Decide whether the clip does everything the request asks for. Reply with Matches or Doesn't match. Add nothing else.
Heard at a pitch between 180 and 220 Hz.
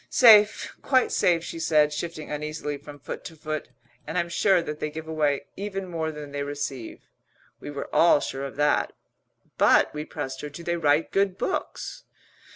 Doesn't match